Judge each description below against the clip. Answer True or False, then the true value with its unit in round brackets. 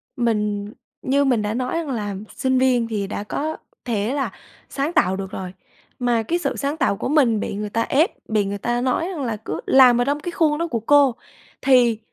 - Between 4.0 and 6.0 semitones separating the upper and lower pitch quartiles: True (4.9 semitones)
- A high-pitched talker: True (245 Hz)